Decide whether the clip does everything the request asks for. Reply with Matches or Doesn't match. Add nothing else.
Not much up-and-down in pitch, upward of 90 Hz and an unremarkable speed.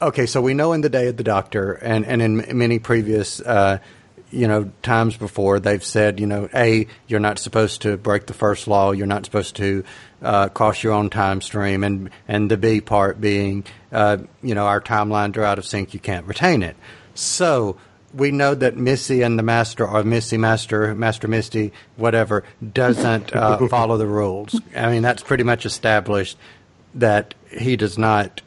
Matches